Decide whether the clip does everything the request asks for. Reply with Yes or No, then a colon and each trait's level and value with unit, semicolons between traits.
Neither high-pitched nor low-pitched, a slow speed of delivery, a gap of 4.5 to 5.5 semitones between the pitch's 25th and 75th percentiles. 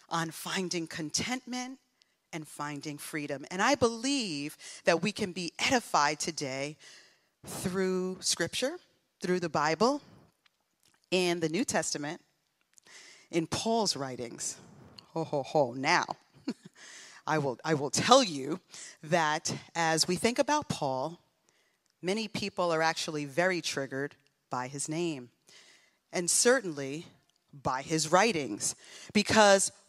Yes: medium, 170 Hz; slow, 115 wpm; average, 5.2 semitones